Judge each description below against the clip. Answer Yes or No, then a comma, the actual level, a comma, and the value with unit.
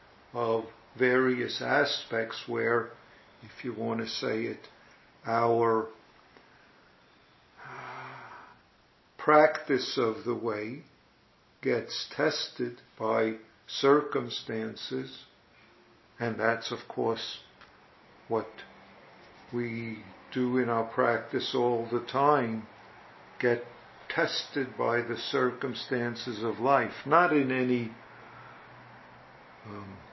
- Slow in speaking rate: Yes, slow, 85 wpm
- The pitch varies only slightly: Yes, narrow, 2.0 semitones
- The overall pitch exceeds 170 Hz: No, low, 120 Hz